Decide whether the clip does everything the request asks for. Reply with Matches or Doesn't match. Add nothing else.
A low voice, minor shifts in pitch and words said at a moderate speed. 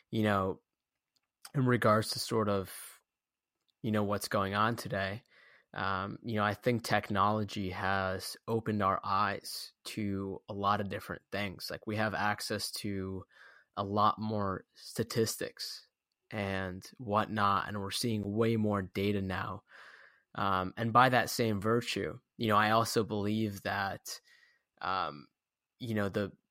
Matches